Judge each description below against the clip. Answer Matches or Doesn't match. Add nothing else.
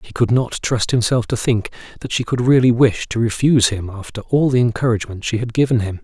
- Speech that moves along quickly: Matches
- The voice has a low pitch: Matches